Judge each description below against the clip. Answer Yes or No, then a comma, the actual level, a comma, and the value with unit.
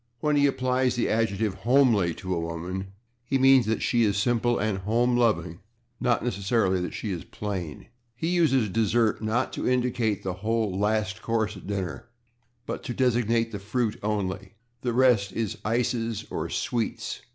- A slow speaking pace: No, average, 165 wpm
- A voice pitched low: Yes, low, 110 Hz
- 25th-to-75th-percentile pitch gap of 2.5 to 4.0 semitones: Yes, average, 3.5 semitones